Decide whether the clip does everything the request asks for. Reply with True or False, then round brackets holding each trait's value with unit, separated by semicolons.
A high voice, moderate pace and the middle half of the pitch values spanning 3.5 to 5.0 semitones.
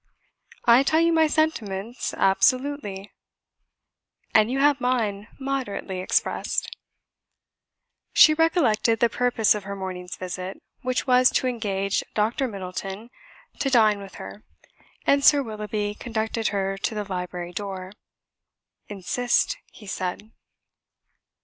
False (215 Hz; 120 wpm; 4.7 semitones)